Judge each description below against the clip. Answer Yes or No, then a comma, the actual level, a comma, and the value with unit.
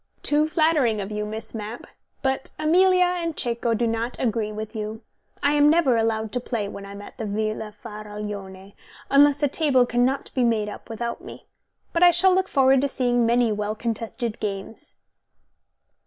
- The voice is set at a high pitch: Yes, high, 235 Hz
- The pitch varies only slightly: No, average, 4.8 semitones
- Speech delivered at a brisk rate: No, average, 180 wpm